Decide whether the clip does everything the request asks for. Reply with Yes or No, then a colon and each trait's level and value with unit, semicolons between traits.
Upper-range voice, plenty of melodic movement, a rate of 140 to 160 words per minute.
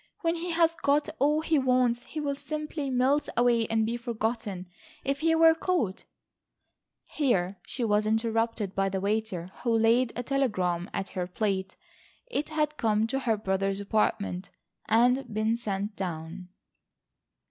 Yes: high, 230 Hz; wide, 5.7 semitones; average, 150 wpm